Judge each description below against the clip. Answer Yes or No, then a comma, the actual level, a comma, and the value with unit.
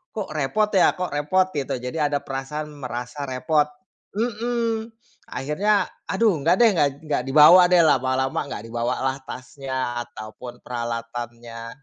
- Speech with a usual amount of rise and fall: No, wide, 6.3 semitones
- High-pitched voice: No, medium, 140 Hz